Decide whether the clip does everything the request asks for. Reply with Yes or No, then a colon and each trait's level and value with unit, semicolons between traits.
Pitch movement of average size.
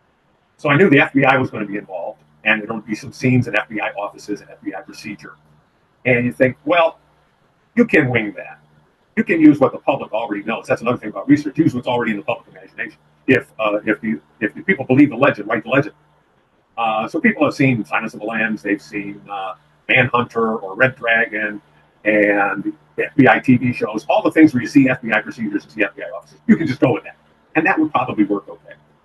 Yes: average, 5.0 semitones